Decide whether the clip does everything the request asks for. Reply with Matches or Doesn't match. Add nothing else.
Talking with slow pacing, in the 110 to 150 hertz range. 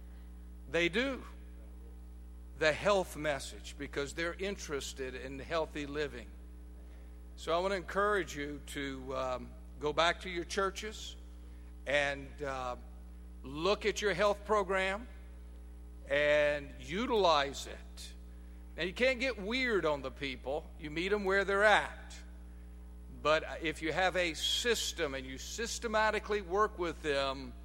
Matches